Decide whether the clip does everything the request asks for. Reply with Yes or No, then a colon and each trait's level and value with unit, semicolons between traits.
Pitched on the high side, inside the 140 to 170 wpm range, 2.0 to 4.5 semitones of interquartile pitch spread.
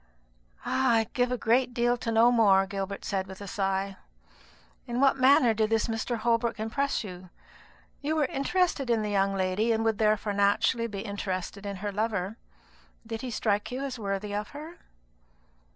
No: high, 220 Hz; average, 180 wpm; average, 3.4 semitones